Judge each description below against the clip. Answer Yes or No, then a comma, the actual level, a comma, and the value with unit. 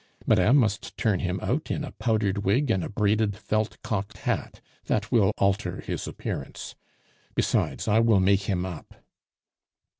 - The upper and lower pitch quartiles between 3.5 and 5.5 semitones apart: No, narrow, 2.6 semitones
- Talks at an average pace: Yes, average, 155 wpm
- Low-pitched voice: Yes, low, 105 Hz